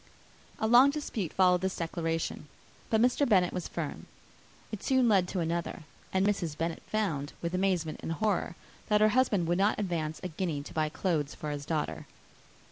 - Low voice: No, medium, 180 Hz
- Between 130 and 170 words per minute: No, average, 180 wpm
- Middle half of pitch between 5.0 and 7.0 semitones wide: No, average, 4.3 semitones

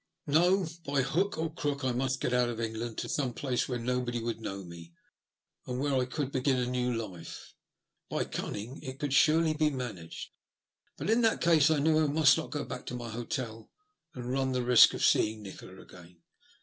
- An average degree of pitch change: Yes, average, 3.9 semitones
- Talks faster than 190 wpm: Yes, average, 200 wpm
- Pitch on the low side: Yes, low, 125 Hz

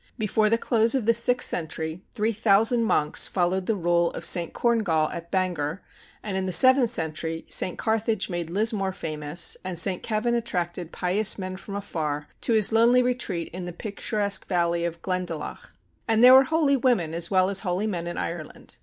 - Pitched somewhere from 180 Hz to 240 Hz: Yes, high, 190 Hz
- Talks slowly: No, average, 180 wpm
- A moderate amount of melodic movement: Yes, average, 4.7 semitones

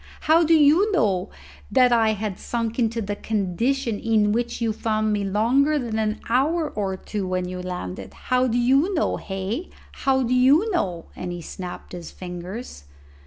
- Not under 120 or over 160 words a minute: No, average, 175 wpm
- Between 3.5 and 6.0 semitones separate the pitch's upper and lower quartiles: Yes, wide, 5.4 semitones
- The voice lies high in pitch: Yes, high, 225 Hz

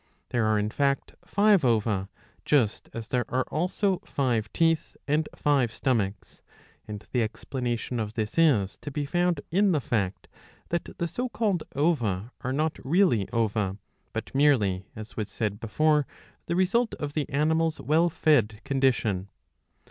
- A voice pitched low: Yes, low, 130 Hz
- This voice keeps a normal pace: Yes, average, 155 wpm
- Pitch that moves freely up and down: Yes, wide, 6.6 semitones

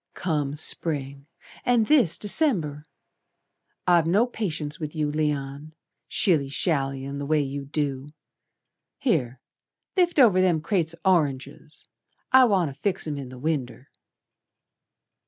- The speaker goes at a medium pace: No, slow, 120 wpm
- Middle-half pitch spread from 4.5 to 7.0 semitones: Yes, average, 4.8 semitones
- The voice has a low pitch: No, medium, 155 Hz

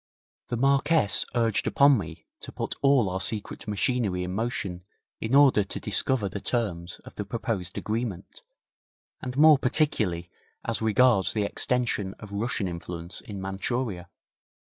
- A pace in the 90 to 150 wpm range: Yes, average, 140 wpm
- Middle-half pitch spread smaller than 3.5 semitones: No, average, 4.8 semitones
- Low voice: Yes, low, 110 Hz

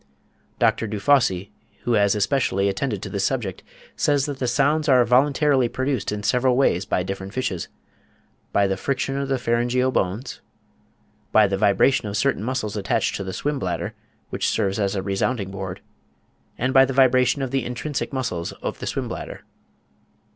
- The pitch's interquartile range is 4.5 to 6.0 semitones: Yes, average, 5.1 semitones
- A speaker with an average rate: Yes, average, 165 wpm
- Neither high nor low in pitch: No, low, 120 Hz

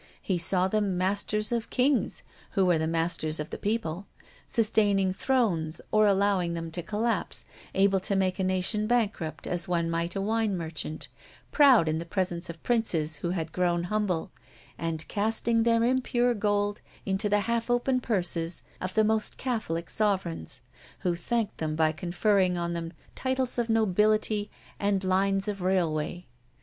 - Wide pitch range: No, average, 4.1 semitones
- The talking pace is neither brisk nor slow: Yes, average, 160 wpm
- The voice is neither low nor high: No, high, 195 Hz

